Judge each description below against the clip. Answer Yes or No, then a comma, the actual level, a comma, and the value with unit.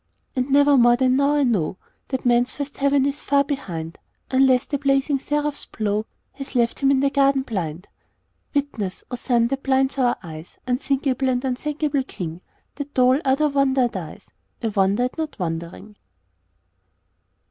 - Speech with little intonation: No, average, 3.3 semitones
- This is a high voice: Yes, very high, 265 Hz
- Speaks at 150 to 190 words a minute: Yes, average, 165 wpm